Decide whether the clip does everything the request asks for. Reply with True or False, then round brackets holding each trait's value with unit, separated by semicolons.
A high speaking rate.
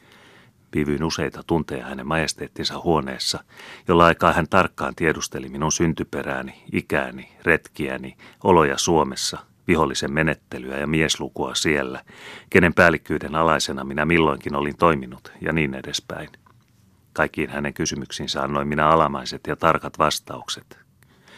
False (115 wpm)